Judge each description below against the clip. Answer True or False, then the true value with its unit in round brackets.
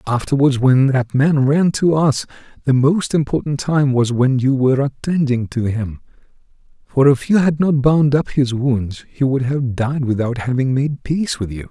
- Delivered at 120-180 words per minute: False (190 wpm)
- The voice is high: False (135 Hz)